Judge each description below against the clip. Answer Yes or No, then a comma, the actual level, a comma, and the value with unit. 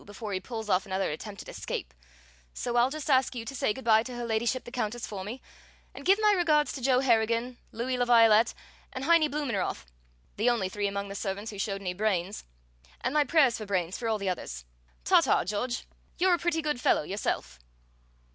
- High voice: Yes, high, 230 Hz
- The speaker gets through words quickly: Yes, fast, 210 wpm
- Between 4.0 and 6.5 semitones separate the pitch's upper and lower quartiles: Yes, average, 4.4 semitones